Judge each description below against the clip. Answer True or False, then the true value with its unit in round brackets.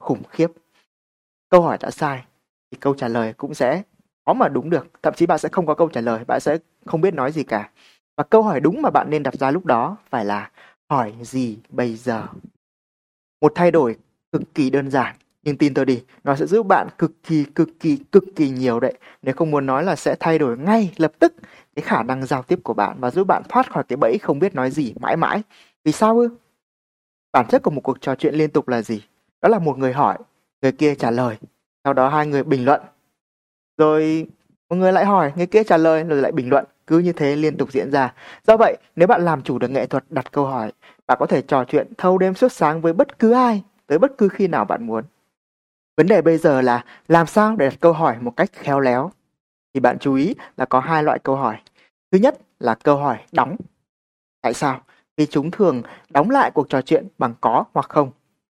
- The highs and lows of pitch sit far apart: False (4.9 semitones)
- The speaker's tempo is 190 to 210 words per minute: False (235 wpm)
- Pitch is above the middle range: False (150 Hz)